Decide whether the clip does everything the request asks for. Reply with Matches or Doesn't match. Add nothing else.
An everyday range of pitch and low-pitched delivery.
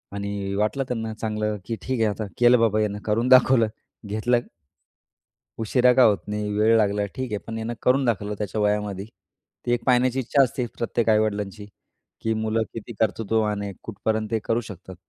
Doesn't match